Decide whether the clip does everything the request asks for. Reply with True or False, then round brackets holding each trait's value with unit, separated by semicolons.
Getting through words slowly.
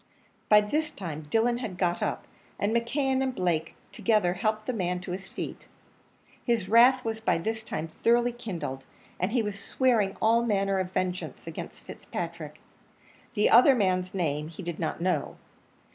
False (170 wpm)